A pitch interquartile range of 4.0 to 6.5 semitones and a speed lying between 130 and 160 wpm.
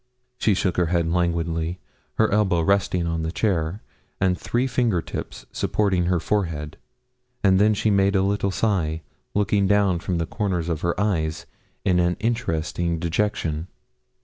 No: average, 3.4 semitones; average, 155 wpm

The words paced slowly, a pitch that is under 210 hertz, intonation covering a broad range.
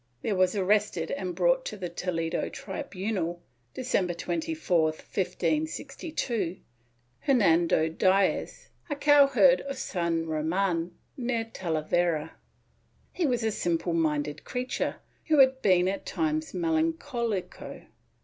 Yes: slow, 110 wpm; high, 190 Hz; wide, 7.7 semitones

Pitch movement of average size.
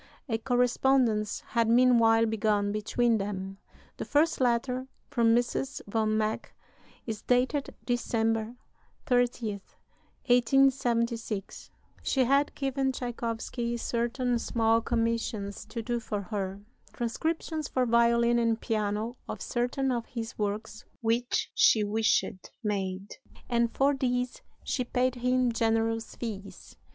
No: narrow, 2.1 semitones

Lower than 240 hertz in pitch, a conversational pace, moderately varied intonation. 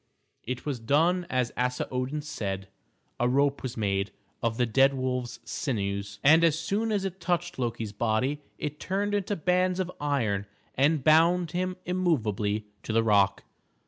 No: low, 135 Hz; average, 160 wpm; wide, 7.2 semitones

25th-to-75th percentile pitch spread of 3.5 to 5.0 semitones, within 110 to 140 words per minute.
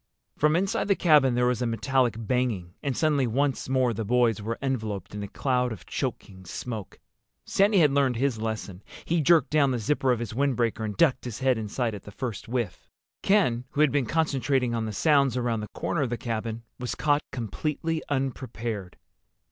No: average, 3.9 semitones; average, 195 wpm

